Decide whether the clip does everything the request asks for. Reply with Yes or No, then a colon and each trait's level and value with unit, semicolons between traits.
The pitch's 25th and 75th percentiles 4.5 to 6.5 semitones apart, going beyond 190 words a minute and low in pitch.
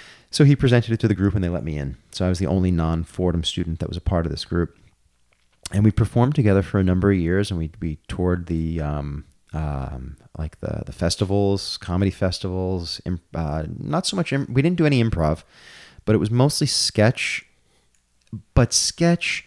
Yes: average, 5.0 semitones; fast, 205 wpm; very low, 95 Hz